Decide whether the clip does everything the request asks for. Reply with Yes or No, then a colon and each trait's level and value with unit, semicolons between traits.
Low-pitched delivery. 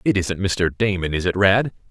Yes: very low, 95 Hz